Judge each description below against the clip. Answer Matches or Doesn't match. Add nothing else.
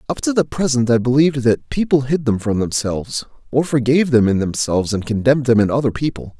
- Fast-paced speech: Matches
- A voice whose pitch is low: Matches